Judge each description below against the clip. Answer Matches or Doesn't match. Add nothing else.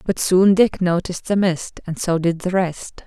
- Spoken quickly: Matches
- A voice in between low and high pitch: Matches